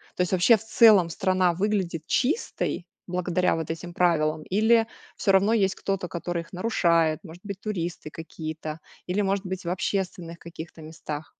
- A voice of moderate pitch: Yes, medium, 180 Hz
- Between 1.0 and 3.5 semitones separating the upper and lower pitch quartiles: Yes, average, 2.9 semitones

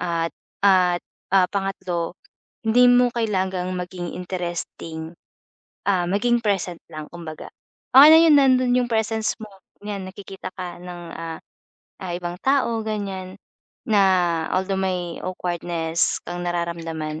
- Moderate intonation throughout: Yes, average, 3.2 semitones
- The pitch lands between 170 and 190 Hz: Yes, medium, 185 Hz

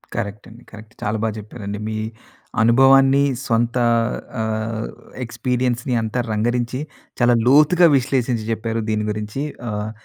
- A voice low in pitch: Yes, low, 115 Hz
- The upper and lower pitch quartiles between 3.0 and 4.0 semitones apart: No, narrow, 2.5 semitones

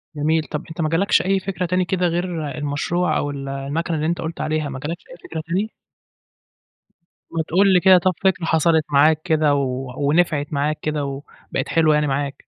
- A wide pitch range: No, average, 3.3 semitones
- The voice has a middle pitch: Yes, medium, 155 Hz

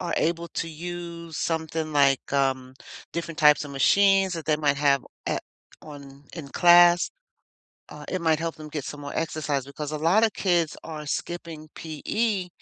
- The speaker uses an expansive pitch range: No, average, 2.8 semitones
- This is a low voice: No, medium, 160 Hz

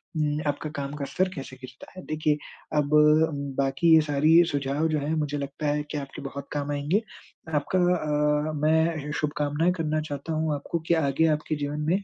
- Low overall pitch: No, medium, 150 Hz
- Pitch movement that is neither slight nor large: No, narrow, 1.6 semitones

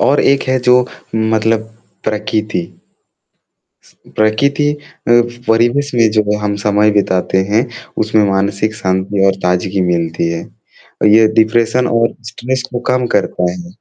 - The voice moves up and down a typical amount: Yes, average, 3.4 semitones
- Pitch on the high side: No, low, 110 Hz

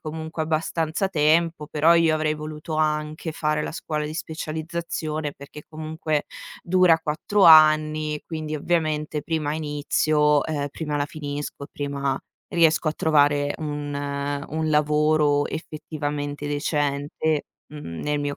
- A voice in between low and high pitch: Yes, medium, 155 Hz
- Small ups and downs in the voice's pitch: Yes, narrow, 1.3 semitones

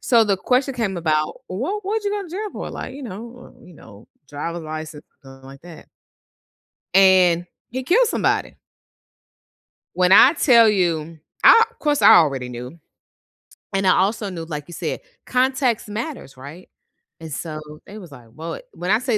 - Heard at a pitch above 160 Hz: Yes, medium, 185 Hz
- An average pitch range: No, wide, 8.0 semitones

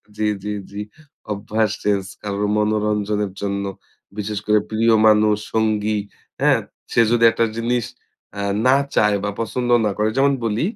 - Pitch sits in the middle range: No, low, 105 Hz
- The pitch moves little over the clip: Yes, narrow, 1.2 semitones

